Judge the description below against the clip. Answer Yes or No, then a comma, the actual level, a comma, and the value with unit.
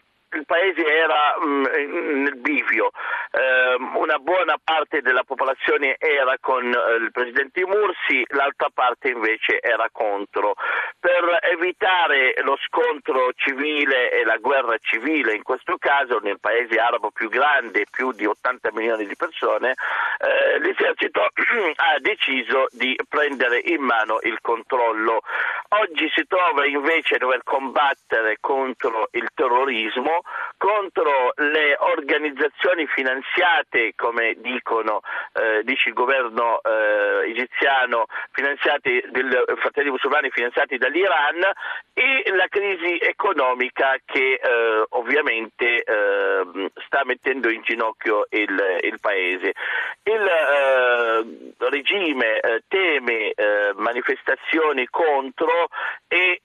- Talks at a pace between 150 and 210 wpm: No, slow, 115 wpm